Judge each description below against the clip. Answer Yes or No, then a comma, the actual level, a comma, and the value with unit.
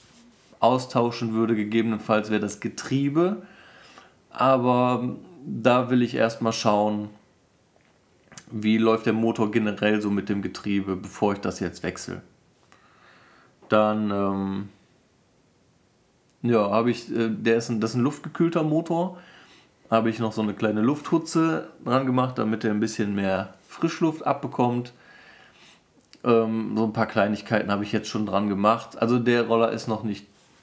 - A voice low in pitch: Yes, low, 115 Hz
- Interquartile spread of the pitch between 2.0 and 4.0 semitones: Yes, average, 2.9 semitones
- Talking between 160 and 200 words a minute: No, average, 145 wpm